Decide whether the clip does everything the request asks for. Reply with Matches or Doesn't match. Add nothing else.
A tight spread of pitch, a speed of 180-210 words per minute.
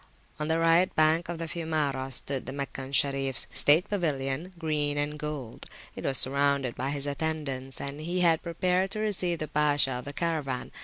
Doesn't match